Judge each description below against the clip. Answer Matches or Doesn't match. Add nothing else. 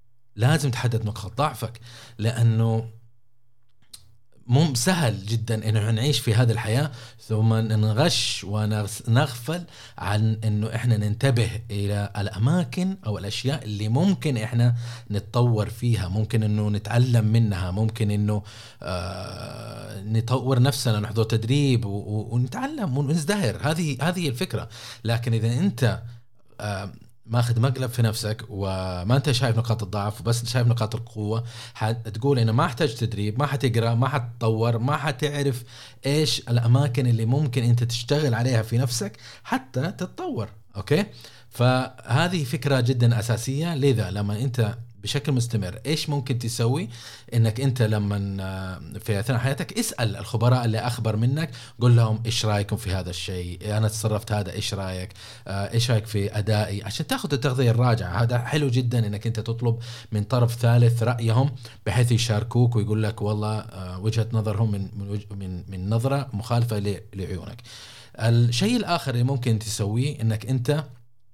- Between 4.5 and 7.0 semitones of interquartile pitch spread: Doesn't match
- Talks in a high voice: Doesn't match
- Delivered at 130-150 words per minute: Matches